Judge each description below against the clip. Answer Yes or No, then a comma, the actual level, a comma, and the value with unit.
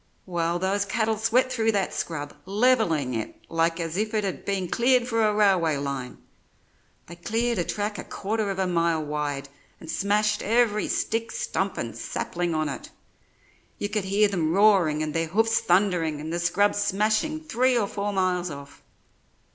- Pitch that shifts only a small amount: No, average, 4.6 semitones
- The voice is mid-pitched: No, high, 195 Hz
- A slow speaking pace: No, average, 175 wpm